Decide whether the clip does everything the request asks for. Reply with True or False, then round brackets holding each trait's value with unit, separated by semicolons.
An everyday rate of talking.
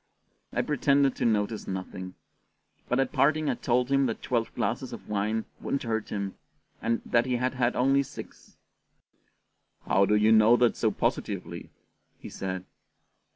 True (155 wpm)